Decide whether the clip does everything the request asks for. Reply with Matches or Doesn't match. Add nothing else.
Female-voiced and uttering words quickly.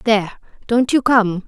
Doesn't match